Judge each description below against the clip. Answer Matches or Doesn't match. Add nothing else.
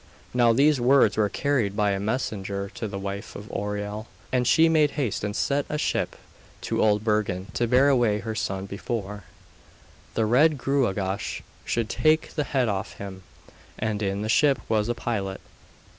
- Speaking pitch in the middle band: Doesn't match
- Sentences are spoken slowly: Doesn't match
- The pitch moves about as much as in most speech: Matches